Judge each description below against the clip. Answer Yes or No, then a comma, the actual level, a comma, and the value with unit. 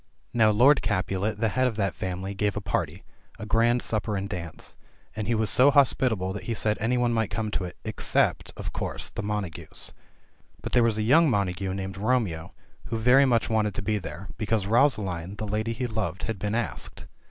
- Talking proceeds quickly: Yes, fast, 215 wpm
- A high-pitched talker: No, low, 105 Hz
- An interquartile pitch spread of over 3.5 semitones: No, average, 3.1 semitones